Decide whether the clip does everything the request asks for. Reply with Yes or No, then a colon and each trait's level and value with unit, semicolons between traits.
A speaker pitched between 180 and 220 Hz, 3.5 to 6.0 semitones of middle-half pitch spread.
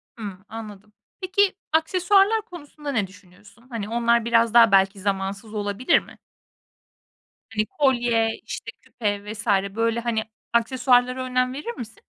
No: high, 230 Hz; average, 3.8 semitones